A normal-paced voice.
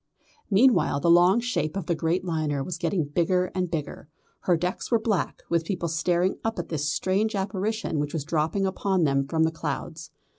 Yes: average, 190 wpm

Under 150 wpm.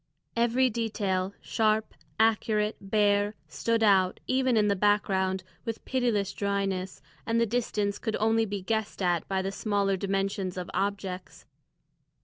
Yes: slow, 135 wpm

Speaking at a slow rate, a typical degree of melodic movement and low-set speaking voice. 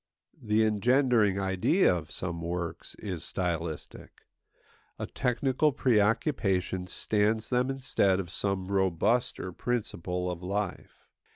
Yes: slow, 105 wpm; average, 5.0 semitones; low, 100 Hz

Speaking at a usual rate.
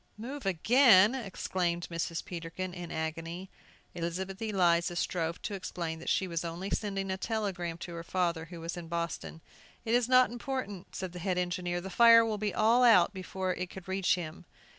Yes: average, 185 wpm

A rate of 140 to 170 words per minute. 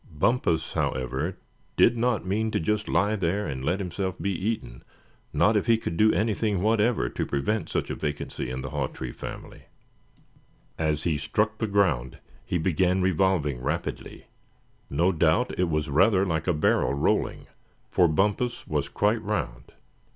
Yes: average, 160 wpm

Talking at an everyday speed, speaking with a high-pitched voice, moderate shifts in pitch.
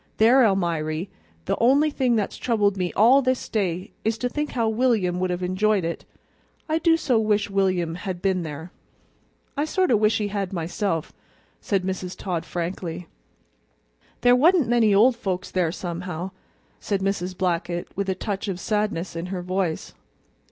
Yes: average, 165 wpm; high, 195 Hz; average, 4.1 semitones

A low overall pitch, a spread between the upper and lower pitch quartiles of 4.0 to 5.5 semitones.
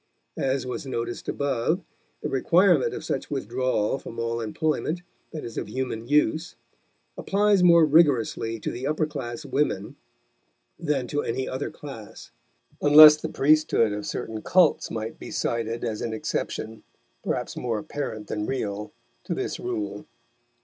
Yes: low, 130 Hz; average, 5.0 semitones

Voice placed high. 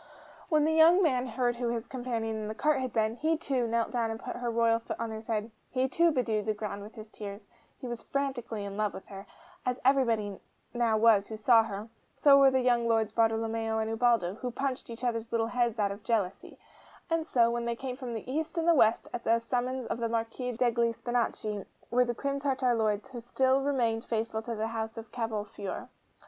Yes: high, 230 Hz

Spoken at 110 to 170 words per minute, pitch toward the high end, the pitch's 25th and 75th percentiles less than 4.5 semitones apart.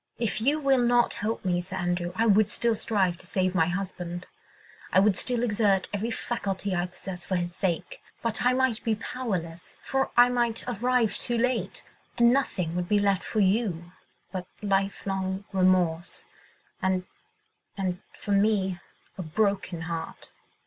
Yes: average, 160 wpm; high, 195 Hz; average, 4.1 semitones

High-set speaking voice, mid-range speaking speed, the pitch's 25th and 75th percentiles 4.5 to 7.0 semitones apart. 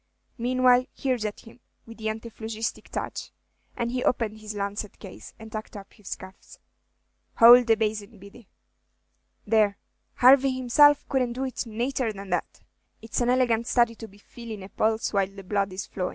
No: high, 225 Hz; average, 170 wpm; average, 3.0 semitones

